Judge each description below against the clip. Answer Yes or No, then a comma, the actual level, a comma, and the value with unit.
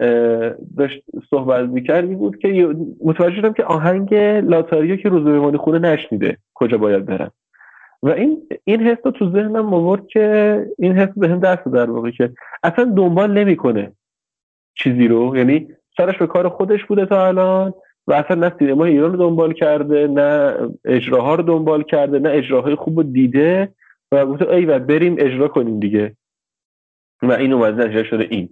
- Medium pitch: Yes, medium, 160 Hz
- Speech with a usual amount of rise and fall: No, wide, 6.4 semitones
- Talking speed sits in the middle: No, fast, 165 wpm